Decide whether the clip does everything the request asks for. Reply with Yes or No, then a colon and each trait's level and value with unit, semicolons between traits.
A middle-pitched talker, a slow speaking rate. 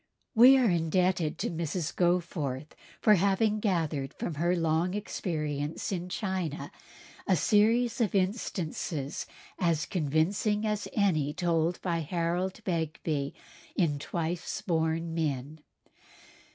Yes: medium, 170 Hz; slow, 110 wpm